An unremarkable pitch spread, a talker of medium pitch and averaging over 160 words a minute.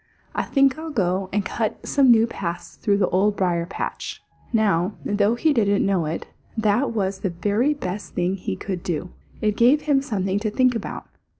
No: average, 4.1 semitones; high, 205 Hz; average, 190 wpm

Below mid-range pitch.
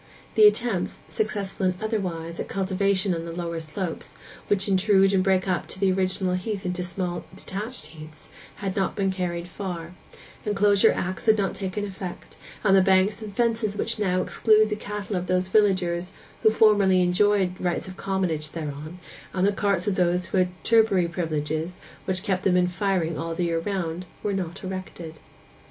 No: medium, 185 Hz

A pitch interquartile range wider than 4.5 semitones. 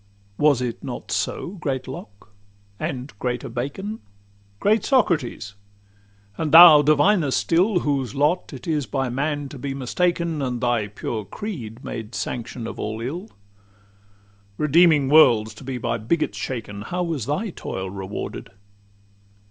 Yes: wide, 5.5 semitones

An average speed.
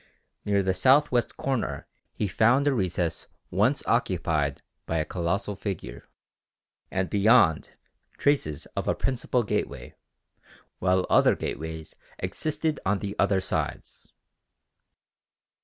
No: slow, 115 wpm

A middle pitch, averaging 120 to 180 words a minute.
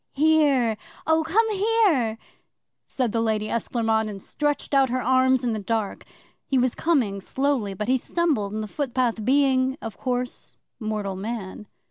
No: very high, 250 Hz; average, 155 wpm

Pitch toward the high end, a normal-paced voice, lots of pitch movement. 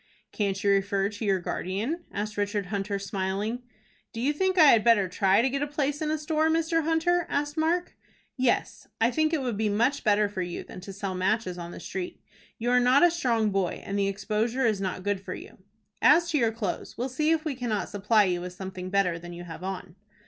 No: high, 215 Hz; fast, 230 wpm; wide, 6.6 semitones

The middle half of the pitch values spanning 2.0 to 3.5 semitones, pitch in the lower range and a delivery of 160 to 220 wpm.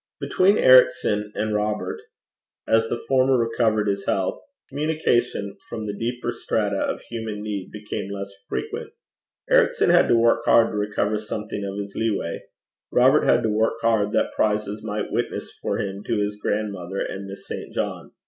Yes: narrow, 2.5 semitones; low, 105 Hz; average, 165 wpm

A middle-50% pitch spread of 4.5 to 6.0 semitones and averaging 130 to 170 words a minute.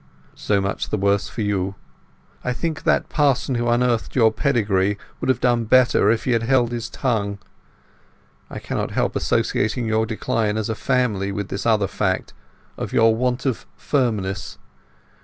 No: average, 3.4 semitones; average, 160 wpm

